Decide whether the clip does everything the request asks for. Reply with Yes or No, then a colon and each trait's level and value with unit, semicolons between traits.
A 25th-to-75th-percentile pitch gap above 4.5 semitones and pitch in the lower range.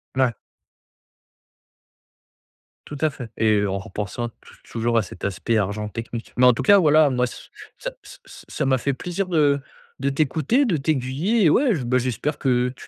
Yes: average, 5.0 semitones; low, 130 Hz